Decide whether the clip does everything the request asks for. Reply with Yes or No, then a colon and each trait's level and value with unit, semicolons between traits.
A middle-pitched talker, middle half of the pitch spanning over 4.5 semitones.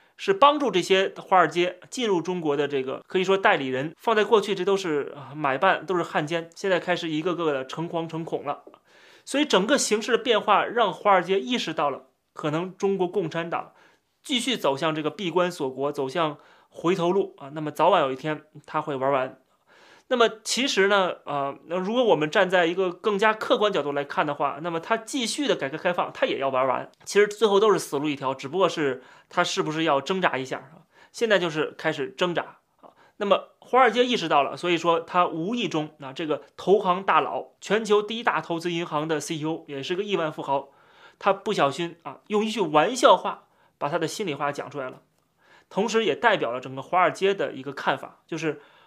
Yes: medium, 175 Hz; average, 5.1 semitones